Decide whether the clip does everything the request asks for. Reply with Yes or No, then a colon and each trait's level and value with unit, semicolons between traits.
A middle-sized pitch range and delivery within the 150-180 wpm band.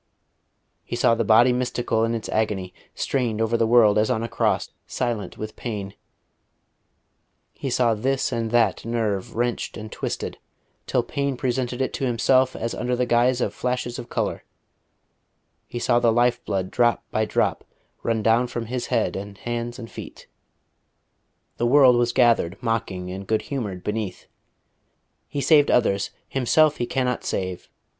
No: narrow, 2.3 semitones; average, 160 wpm